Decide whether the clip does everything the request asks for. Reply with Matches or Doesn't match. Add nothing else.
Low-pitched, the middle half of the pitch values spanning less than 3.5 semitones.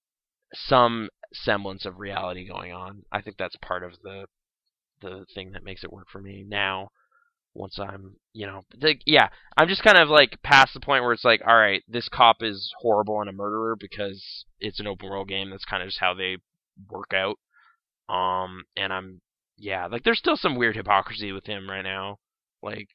Matches